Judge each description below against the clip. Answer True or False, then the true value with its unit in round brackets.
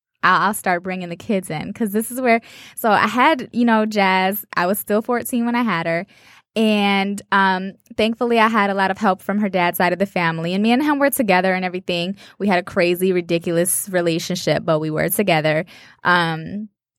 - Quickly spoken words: True (210 wpm)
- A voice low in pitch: False (195 Hz)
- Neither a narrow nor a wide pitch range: True (3.6 semitones)